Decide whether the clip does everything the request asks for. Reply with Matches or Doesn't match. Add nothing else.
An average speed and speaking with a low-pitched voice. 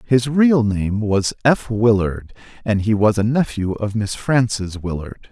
Matches